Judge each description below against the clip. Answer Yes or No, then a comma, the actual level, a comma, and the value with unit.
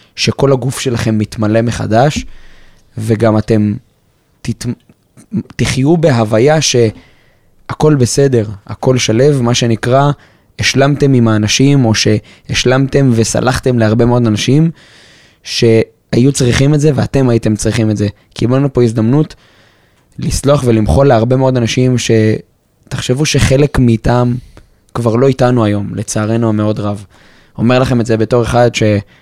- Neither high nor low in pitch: No, low, 120 Hz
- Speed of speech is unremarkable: Yes, average, 120 wpm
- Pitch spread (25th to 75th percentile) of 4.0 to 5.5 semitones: No, average, 3.2 semitones